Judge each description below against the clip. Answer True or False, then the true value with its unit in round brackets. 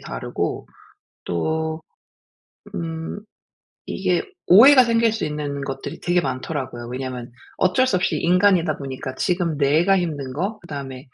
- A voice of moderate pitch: True (160 Hz)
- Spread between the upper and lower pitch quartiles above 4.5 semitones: True (5.2 semitones)